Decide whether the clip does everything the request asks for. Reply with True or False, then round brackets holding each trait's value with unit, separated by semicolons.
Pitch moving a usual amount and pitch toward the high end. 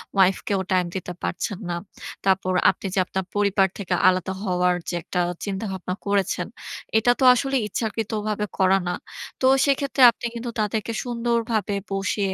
True (3.0 semitones; 200 Hz)